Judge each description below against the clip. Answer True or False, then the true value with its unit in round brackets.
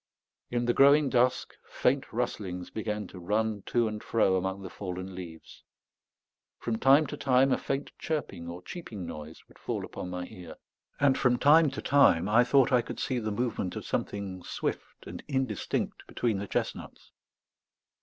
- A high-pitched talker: False (110 Hz)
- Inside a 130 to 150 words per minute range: False (170 wpm)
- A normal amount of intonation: False (6.0 semitones)